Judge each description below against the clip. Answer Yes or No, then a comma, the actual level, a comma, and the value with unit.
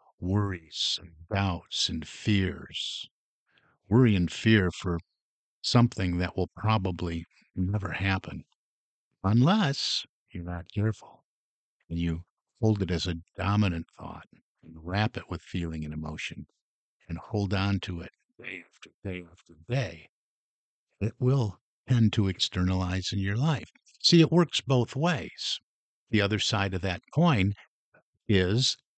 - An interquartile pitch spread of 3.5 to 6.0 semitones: Yes, average, 3.9 semitones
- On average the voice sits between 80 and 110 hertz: Yes, very low, 95 Hz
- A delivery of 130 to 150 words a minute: Yes, slow, 135 wpm